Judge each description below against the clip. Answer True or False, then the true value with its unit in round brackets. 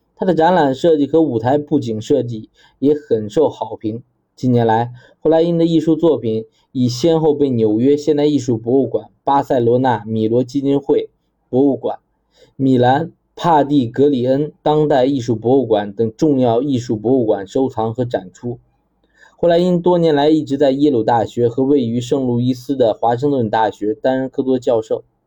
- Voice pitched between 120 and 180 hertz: True (135 Hz)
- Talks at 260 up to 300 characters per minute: True (270 characters per minute)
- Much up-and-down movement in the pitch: False (3.8 semitones)